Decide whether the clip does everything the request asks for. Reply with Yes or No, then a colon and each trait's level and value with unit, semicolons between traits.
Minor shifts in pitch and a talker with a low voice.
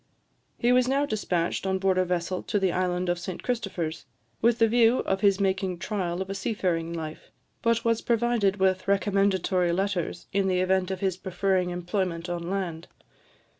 No: narrow, 2.3 semitones; high, 190 Hz